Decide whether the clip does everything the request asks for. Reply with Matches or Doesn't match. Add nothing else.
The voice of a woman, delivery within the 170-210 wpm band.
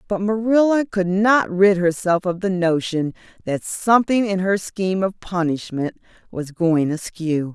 Doesn't match